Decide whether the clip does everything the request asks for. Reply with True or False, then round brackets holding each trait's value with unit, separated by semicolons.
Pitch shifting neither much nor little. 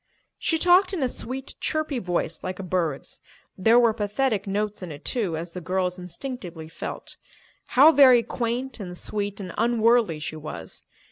False (5.8 semitones)